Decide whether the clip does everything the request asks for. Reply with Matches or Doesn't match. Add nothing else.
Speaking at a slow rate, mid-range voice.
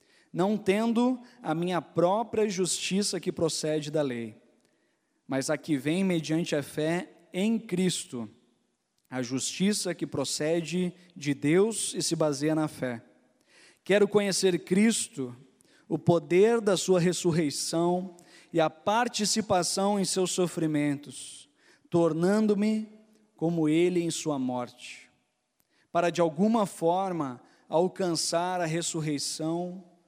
Matches